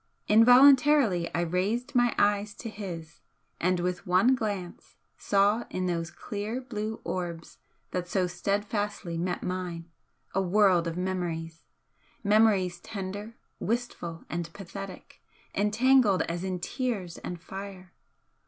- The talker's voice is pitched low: No, high, 190 Hz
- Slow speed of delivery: Yes, slow, 120 wpm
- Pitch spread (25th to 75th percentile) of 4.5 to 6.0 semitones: No, average, 3.5 semitones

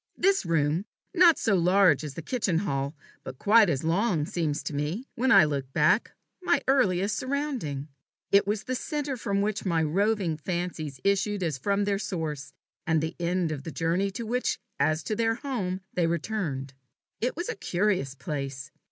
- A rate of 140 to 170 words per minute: No, average, 180 wpm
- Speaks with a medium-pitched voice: Yes, medium, 180 Hz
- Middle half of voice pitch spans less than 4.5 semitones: No, wide, 5.6 semitones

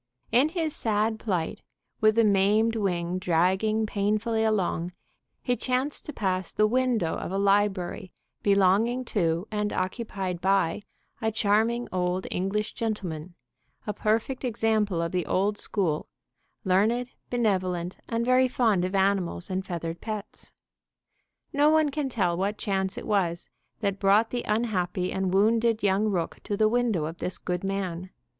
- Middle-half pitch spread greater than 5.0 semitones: No, average, 3.4 semitones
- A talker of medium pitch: No, high, 205 Hz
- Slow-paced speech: No, average, 150 wpm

